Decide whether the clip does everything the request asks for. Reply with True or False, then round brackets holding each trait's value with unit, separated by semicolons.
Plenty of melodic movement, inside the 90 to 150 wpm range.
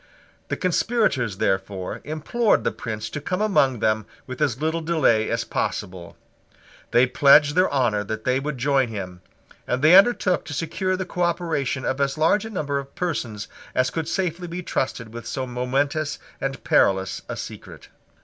False (6.0 semitones; 170 wpm)